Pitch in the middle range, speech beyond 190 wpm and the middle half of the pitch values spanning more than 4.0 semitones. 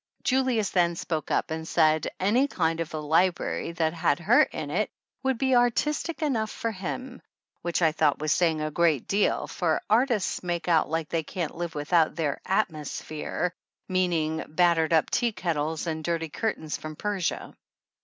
No: medium, 170 Hz; average, 175 wpm; average, 4.4 semitones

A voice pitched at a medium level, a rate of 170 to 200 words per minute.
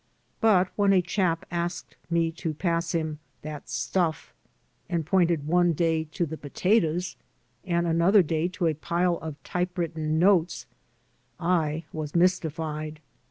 No: medium, 170 Hz; slow, 135 wpm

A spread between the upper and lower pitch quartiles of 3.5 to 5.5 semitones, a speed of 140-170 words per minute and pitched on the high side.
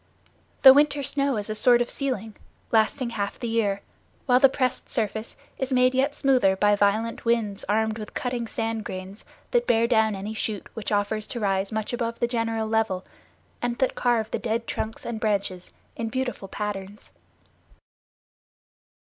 No: average, 2.9 semitones; average, 165 wpm; high, 225 Hz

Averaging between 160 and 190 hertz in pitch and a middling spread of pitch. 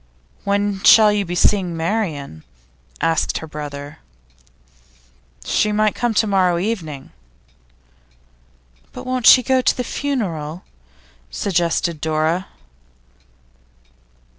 Yes: medium, 185 Hz; average, 5.0 semitones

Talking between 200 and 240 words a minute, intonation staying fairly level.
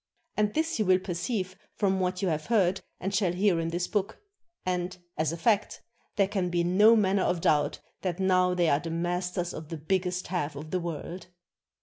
Yes: fast, 205 wpm; narrow, 2.1 semitones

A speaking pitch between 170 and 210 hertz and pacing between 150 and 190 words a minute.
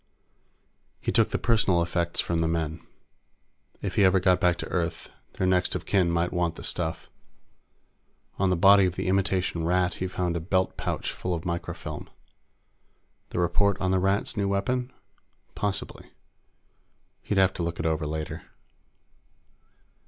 No: very low, 90 Hz; average, 160 wpm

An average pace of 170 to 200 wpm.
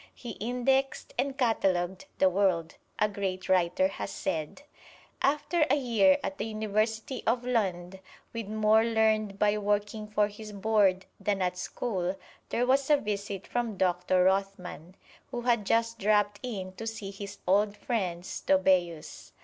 No: average, 150 wpm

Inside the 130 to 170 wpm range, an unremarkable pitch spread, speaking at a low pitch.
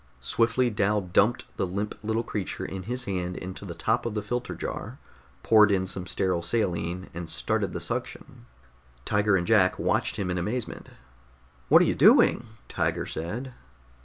Yes: average, 165 wpm; average, 3.7 semitones; low, 100 Hz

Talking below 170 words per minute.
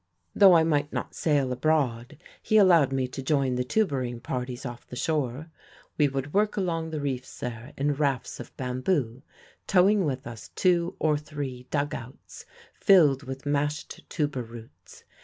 Yes: average, 160 wpm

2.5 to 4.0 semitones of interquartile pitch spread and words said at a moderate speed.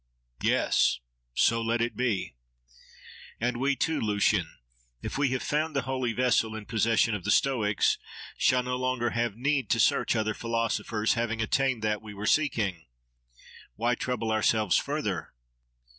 Yes: average, 2.9 semitones; average, 150 wpm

